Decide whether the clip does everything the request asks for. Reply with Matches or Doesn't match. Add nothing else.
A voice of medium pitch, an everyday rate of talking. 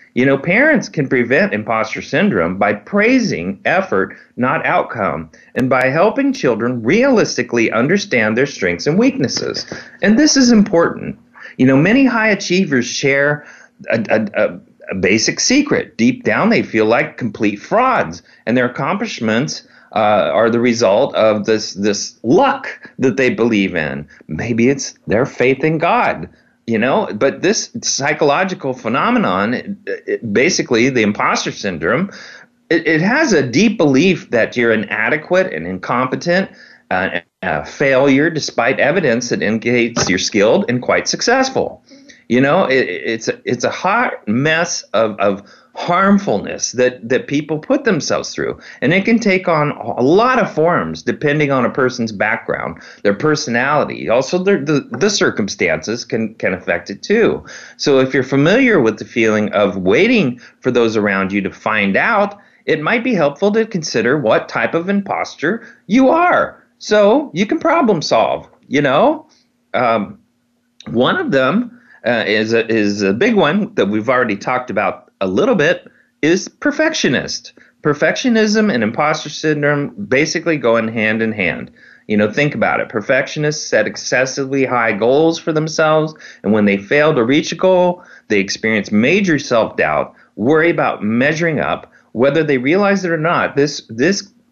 Matches